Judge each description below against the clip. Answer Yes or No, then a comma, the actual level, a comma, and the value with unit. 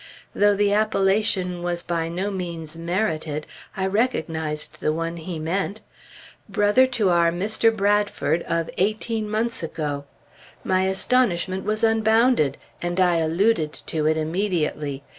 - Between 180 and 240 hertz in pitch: Yes, medium, 185 Hz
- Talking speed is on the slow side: Yes, slow, 130 wpm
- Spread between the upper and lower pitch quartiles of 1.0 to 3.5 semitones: No, average, 4.3 semitones